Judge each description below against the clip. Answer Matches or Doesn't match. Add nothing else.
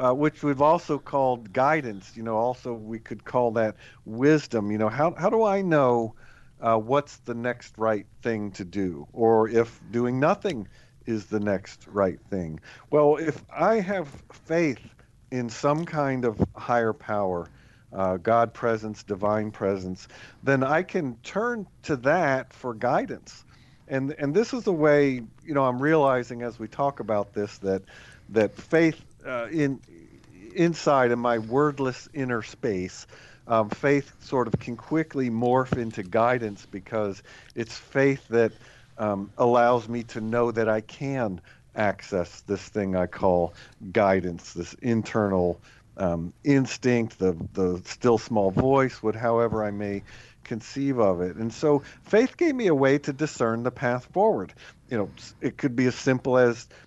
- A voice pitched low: Matches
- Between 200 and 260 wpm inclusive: Doesn't match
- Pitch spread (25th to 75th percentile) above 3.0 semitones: Matches